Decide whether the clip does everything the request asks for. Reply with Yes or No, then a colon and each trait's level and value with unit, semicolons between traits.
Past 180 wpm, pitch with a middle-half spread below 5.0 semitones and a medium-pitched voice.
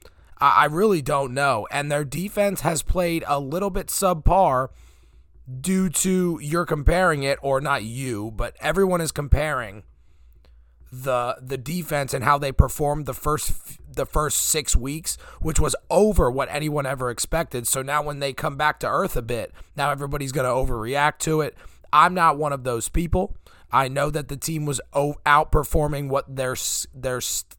No: average, 170 wpm; average, 3.2 semitones; medium, 145 Hz